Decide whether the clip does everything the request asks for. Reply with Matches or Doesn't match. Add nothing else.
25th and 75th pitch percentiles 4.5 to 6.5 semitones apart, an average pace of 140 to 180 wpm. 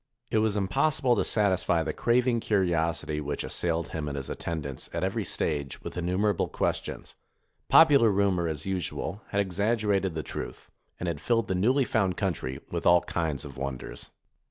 Matches